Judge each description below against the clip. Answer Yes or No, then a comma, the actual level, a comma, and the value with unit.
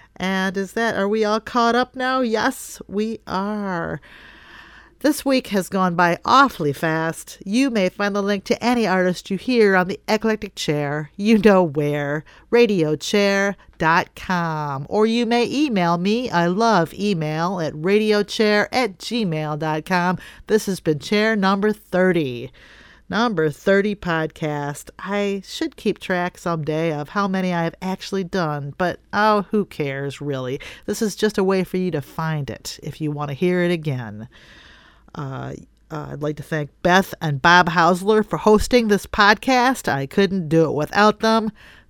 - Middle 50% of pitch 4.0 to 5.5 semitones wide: Yes, average, 5.0 semitones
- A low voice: No, high, 190 Hz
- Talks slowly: No, average, 160 wpm